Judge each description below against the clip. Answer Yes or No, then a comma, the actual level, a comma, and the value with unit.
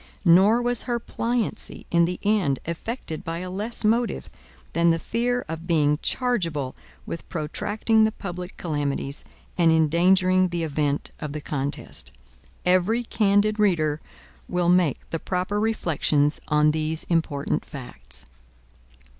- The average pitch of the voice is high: No, medium, 175 Hz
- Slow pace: Yes, slow, 130 wpm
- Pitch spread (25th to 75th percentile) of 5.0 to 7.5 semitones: Yes, average, 5.3 semitones